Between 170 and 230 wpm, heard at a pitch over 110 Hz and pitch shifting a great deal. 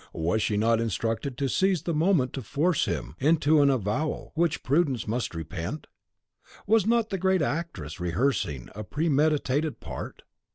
No: average, 155 wpm; medium, 140 Hz; wide, 6.8 semitones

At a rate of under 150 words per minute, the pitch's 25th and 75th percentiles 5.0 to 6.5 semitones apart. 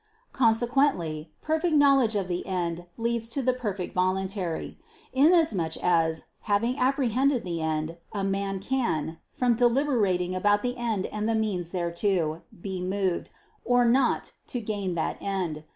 Yes: average, 140 wpm; wide, 5.6 semitones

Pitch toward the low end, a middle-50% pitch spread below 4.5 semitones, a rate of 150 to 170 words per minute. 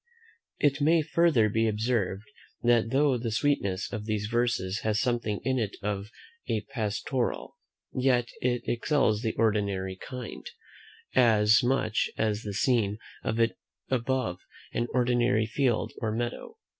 No: low, 115 Hz; average, 3.1 semitones; average, 140 wpm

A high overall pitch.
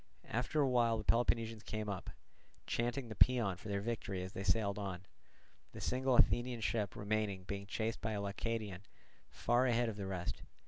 No: low, 110 Hz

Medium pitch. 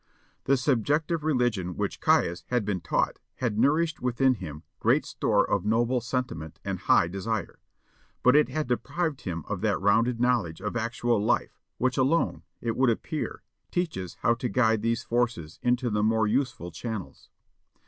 No: low, 120 Hz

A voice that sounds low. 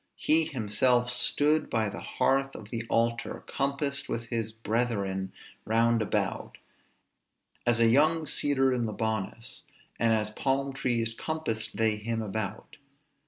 Yes: low, 115 Hz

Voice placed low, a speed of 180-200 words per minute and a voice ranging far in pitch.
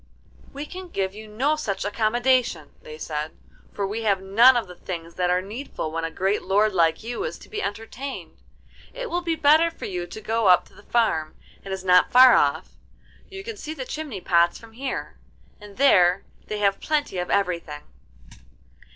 No: high, 210 Hz; average, 195 wpm; wide, 6.4 semitones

